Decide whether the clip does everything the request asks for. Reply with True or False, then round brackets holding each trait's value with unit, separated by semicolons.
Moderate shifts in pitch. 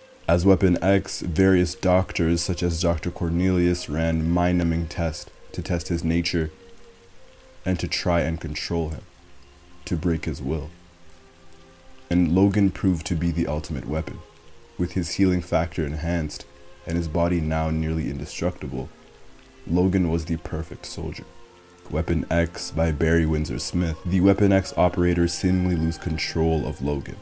False (1.9 semitones)